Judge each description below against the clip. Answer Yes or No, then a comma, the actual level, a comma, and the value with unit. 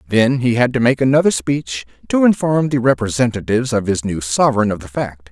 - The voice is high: No, low, 120 Hz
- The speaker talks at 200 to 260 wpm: Yes, fast, 205 wpm